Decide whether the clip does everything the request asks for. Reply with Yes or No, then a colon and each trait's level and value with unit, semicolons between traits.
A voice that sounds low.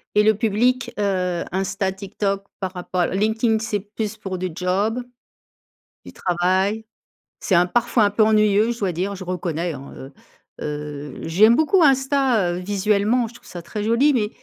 No: high, 200 Hz